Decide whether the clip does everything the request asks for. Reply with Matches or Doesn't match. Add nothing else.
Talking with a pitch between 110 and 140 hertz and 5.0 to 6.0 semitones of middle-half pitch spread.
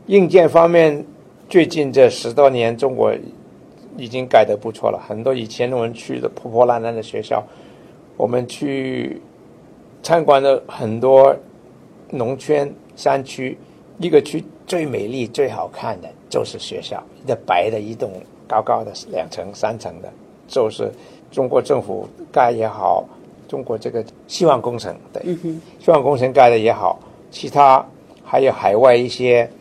Matches